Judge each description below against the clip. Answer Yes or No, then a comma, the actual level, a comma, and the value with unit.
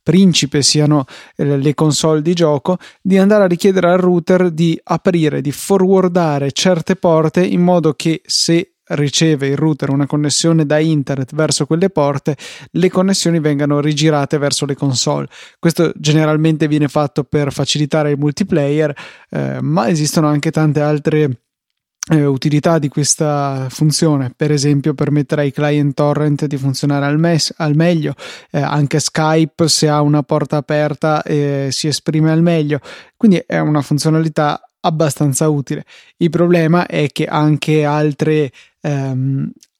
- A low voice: No, medium, 150 Hz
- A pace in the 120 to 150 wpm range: Yes, average, 145 wpm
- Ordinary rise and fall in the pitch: No, narrow, 2.1 semitones